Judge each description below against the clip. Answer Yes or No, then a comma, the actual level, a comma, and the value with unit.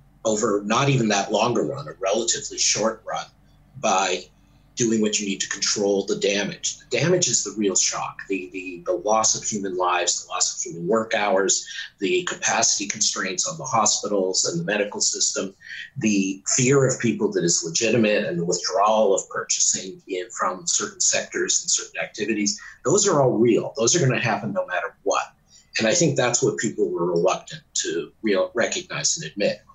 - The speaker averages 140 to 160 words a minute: No, average, 190 wpm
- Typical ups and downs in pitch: No, wide, 5.7 semitones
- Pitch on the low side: Yes, low, 115 Hz